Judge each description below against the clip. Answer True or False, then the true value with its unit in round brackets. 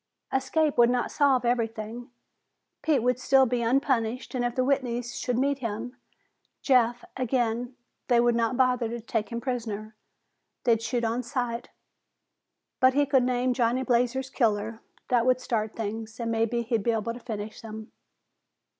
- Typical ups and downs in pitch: False (1.9 semitones)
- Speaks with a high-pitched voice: True (240 Hz)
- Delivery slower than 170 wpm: True (160 wpm)